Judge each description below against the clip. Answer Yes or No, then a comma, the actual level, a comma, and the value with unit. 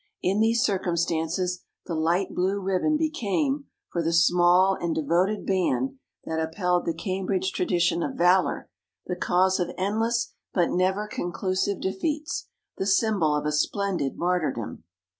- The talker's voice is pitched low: No, medium, 185 Hz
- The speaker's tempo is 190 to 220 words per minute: No, average, 140 wpm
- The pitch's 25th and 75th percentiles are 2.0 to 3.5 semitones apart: Yes, average, 2.7 semitones